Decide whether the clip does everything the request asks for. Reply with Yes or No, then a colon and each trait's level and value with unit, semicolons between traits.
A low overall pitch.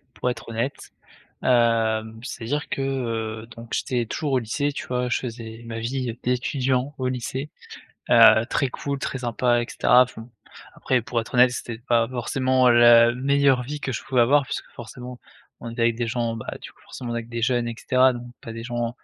Yes: low, 120 Hz